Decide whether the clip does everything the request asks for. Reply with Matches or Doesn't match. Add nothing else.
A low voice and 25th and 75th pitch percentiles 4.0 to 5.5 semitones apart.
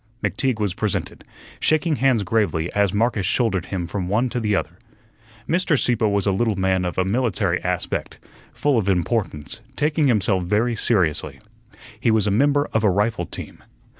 Matches